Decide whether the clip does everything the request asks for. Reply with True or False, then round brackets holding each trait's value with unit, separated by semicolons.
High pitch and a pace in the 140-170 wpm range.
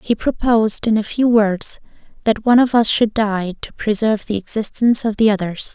False (215 Hz; 200 wpm)